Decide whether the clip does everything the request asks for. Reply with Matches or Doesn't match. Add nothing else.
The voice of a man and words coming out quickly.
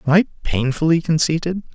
Doesn't match